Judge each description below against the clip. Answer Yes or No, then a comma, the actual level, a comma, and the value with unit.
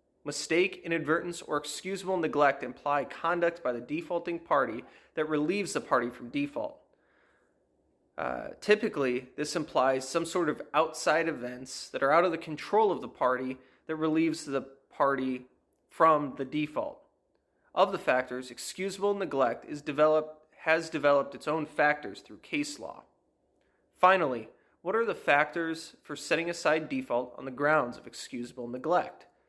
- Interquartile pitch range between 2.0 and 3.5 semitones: No, average, 4.1 semitones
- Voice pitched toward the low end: No, medium, 155 Hz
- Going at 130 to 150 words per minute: Yes, average, 145 wpm